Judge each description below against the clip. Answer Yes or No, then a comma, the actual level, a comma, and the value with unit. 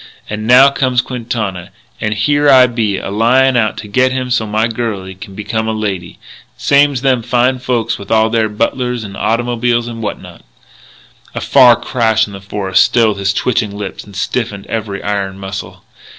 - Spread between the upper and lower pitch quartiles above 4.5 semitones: No, average, 3.3 semitones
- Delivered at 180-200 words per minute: Yes, average, 185 wpm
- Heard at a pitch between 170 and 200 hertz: No, low, 115 Hz